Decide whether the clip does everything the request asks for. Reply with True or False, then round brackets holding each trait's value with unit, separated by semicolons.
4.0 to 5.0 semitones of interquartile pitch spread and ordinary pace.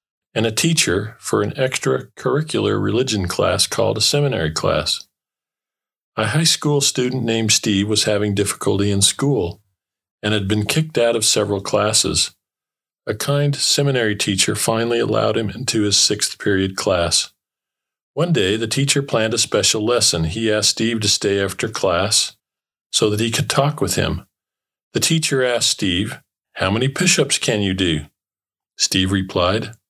True (4.6 semitones; 155 wpm)